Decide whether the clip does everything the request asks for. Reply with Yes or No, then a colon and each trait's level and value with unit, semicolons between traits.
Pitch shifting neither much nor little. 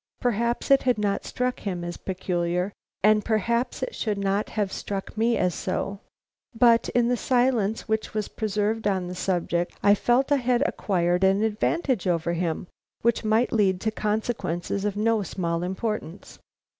Yes: average, 3.8 semitones